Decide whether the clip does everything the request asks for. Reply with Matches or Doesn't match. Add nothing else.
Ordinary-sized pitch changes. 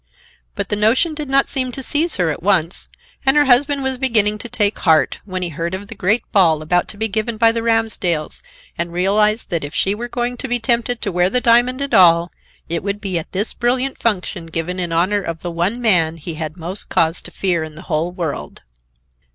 Doesn't match